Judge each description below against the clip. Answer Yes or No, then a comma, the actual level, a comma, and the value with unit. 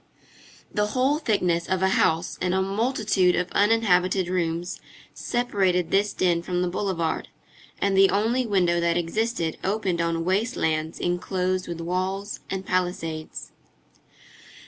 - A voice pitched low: No, medium, 185 Hz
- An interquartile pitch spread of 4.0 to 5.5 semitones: No, average, 2.8 semitones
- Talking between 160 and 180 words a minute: No, slow, 135 wpm